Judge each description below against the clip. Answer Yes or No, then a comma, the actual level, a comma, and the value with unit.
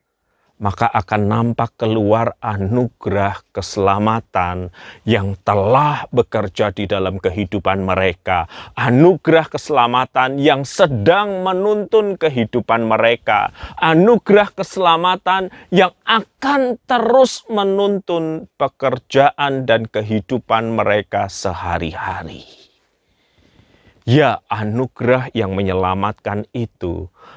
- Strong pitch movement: Yes, wide, 8.0 semitones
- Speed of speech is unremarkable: No, slow, 80 wpm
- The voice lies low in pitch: Yes, low, 115 Hz